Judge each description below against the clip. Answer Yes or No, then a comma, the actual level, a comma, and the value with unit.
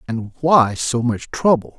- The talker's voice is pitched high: No, low, 130 Hz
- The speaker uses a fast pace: No, average, 170 wpm